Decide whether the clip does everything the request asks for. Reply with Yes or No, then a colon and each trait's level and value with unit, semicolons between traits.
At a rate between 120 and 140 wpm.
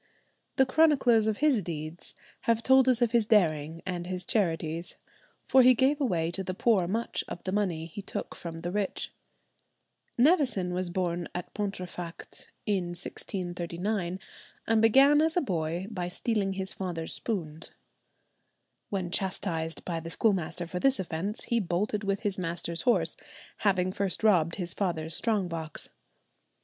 No: average, 155 wpm